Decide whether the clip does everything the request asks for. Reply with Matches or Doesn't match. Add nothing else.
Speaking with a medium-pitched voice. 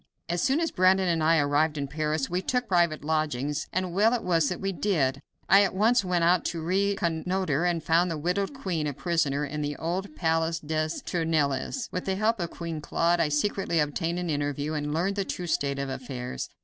Matches